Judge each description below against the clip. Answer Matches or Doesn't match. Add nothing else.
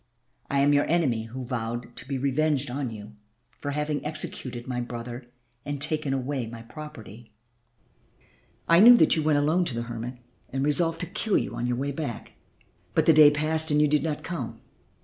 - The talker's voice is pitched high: Doesn't match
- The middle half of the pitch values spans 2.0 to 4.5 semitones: Matches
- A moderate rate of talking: Matches